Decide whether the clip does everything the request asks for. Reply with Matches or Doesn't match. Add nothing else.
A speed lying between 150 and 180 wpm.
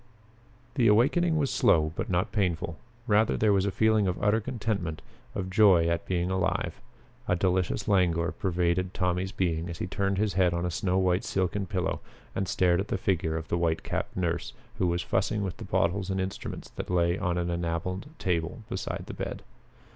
Doesn't match